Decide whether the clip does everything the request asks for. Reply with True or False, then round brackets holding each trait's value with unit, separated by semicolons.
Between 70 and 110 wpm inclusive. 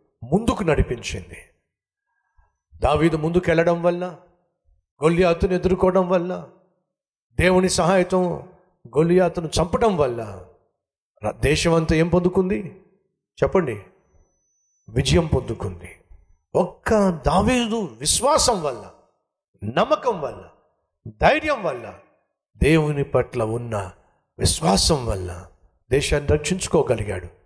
True (75 wpm)